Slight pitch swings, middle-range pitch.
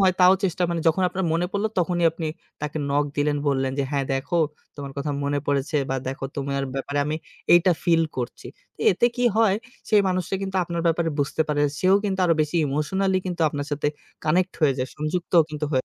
No: average, 4.2 semitones; medium, 160 Hz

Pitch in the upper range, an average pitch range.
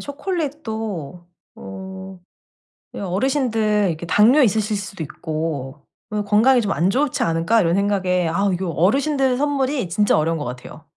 No: high, 200 Hz; wide, 6.4 semitones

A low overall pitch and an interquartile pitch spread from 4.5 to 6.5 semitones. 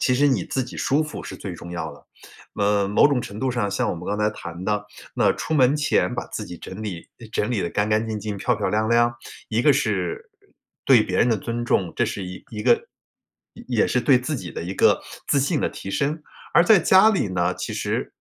Yes: low, 110 Hz; average, 4.9 semitones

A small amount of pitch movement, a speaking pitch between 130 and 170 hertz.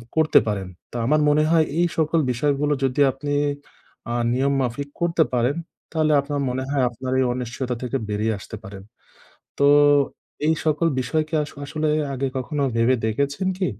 No: average, 3.6 semitones; medium, 140 Hz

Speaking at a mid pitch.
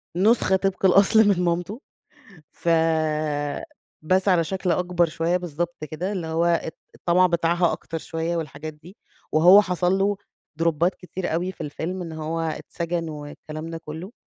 Yes: medium, 175 Hz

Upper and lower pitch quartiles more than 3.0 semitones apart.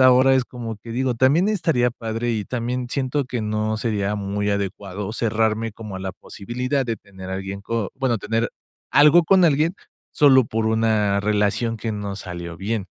Yes: average, 3.7 semitones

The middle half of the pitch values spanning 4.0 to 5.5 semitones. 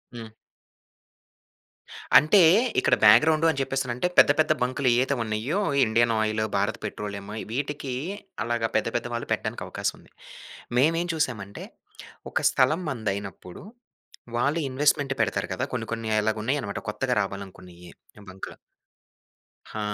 Yes: average, 4.7 semitones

